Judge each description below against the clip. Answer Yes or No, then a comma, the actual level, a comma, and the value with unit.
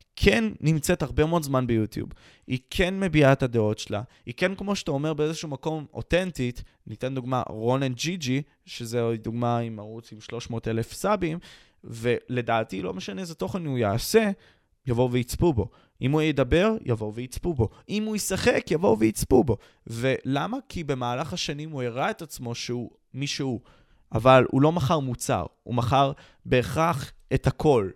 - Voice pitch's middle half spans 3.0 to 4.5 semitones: No, average, 5.1 semitones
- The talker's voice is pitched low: Yes, low, 130 Hz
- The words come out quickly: Yes, fast, 165 wpm